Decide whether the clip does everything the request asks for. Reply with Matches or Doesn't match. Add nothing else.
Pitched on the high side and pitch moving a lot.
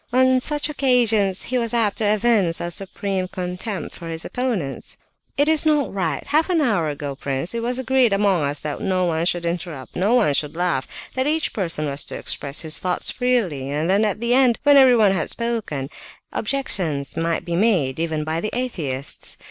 Matches